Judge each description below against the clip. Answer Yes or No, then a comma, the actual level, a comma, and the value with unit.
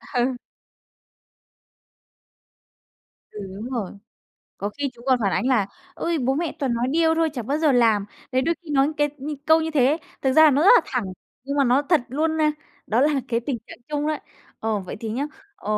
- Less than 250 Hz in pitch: No, very high, 270 Hz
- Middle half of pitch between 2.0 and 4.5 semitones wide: Yes, average, 4.2 semitones